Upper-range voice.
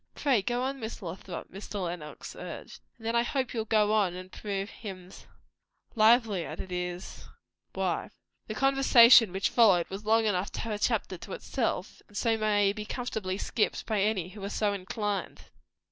Yes: high, 210 Hz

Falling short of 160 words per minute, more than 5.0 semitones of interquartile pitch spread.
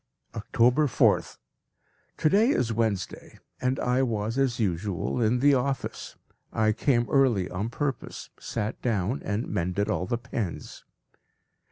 No: slow, 135 wpm; average, 3.8 semitones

